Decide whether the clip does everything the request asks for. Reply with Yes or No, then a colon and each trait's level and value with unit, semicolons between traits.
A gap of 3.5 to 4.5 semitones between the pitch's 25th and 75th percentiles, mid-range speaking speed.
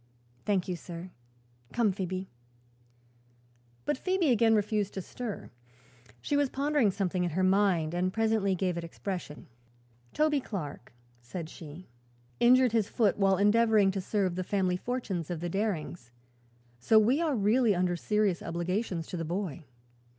Yes: average, 4.0 semitones; average, 150 wpm